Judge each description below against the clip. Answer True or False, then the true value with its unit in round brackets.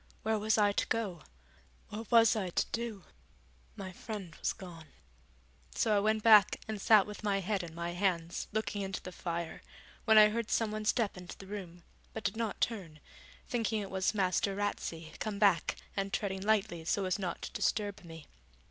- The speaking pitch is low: False (200 Hz)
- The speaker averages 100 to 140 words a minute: False (185 wpm)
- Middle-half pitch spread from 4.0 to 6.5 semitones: False (3.1 semitones)